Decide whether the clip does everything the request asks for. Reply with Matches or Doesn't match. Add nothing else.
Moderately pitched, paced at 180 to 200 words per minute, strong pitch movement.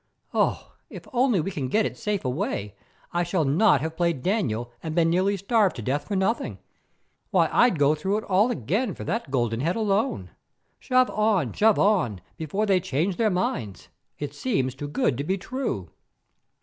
Matches